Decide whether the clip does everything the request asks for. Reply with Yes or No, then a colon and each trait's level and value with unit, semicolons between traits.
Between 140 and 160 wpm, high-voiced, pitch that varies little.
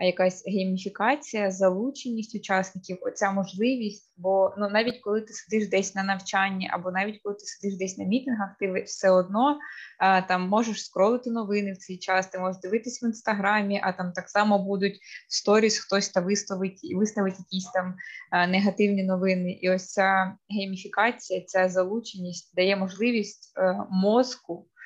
Yes: average, 150 wpm; high, 195 Hz; narrow, 2.1 semitones